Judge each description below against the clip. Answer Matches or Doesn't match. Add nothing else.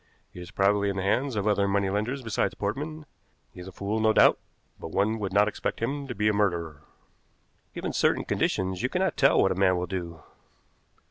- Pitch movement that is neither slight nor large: Matches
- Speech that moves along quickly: Matches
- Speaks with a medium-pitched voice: Doesn't match